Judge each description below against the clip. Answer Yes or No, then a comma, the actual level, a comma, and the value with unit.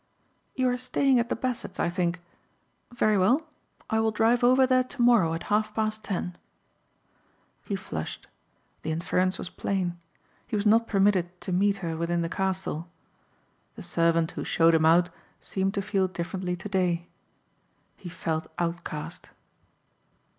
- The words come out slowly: No, average, 145 wpm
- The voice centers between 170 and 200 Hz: Yes, high, 190 Hz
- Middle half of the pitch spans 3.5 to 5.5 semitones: Yes, average, 4.2 semitones